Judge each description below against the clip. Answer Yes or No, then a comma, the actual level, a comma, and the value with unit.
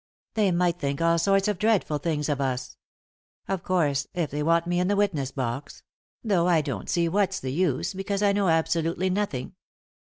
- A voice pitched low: No, medium, 170 Hz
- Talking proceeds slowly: No, average, 190 wpm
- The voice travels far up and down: No, average, 4.6 semitones